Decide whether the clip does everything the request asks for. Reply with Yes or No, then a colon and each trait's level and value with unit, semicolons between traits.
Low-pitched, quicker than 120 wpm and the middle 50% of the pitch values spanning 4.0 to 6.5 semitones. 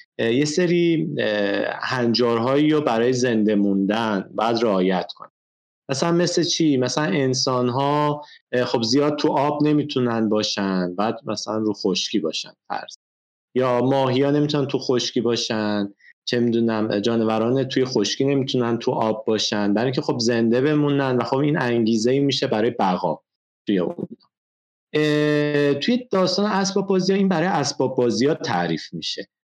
Yes: low, 130 Hz; average, 140 wpm; average, 4.8 semitones